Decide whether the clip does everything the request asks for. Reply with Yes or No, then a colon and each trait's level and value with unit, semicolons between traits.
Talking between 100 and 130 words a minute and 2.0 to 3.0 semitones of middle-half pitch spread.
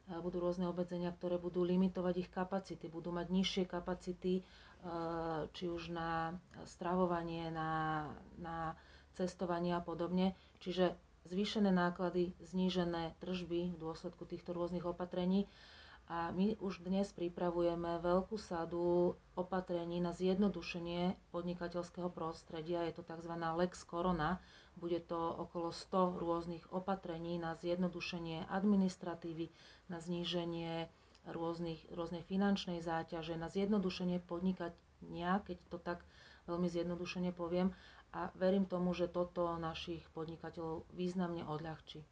No: average, 115 wpm; narrow, 1.2 semitones